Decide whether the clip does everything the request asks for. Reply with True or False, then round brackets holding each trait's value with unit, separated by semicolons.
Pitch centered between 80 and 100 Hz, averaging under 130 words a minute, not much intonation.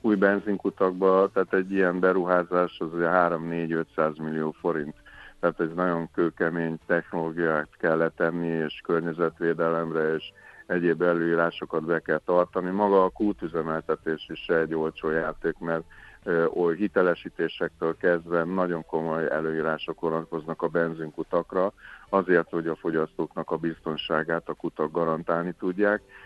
True (85 Hz; 120 wpm; 1.9 semitones)